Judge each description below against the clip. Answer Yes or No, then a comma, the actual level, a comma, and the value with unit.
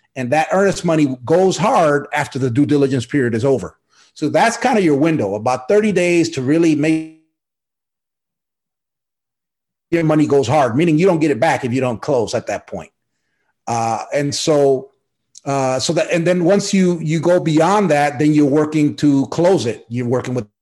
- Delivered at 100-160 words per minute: No, average, 190 wpm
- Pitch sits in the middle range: Yes, medium, 150 Hz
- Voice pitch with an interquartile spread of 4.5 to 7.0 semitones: No, average, 3.7 semitones